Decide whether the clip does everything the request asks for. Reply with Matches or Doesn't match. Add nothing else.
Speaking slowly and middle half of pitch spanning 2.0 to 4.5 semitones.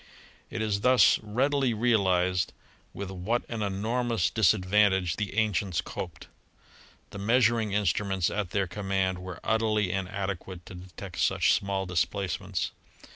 Matches